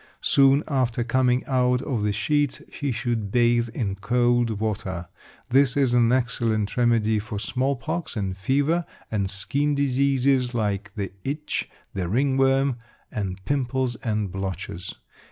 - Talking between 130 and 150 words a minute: Yes, slow, 135 wpm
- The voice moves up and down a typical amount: Yes, average, 4.3 semitones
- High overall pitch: No, low, 120 Hz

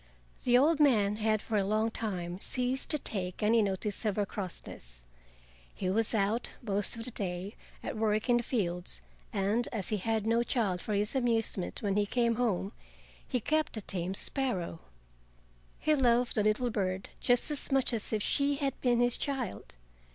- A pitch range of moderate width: Yes, average, 3.7 semitones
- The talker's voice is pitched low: No, high, 220 Hz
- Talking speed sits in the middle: Yes, average, 180 wpm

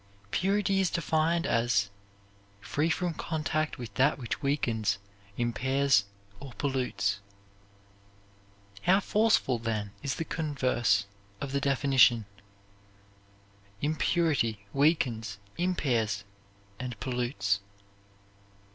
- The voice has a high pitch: No, low, 135 Hz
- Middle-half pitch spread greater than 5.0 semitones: Yes, wide, 5.5 semitones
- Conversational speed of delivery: No, slow, 90 wpm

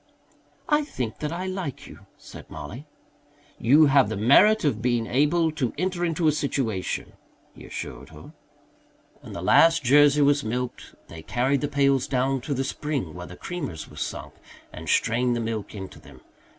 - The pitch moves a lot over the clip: No, average, 4.4 semitones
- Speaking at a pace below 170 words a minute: No, average, 175 wpm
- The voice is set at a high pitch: No, medium, 140 Hz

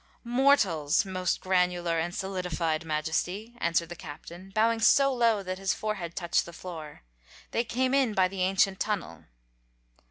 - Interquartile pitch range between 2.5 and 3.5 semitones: No, average, 4.2 semitones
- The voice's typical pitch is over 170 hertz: Yes, medium, 185 Hz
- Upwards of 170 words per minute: No, average, 150 wpm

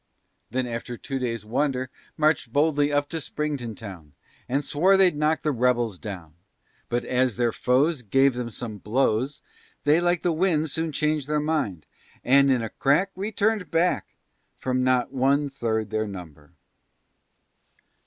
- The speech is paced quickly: No, average, 155 wpm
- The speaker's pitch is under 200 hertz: Yes, low, 135 Hz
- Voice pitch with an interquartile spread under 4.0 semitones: No, average, 4.6 semitones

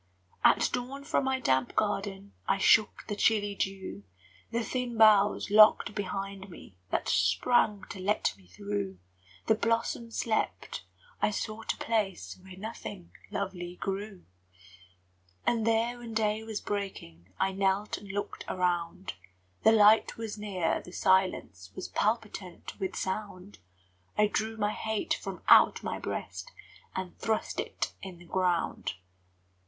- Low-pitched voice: No, high, 205 Hz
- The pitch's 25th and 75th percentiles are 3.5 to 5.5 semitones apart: No, average, 2.9 semitones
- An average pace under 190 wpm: Yes, average, 140 wpm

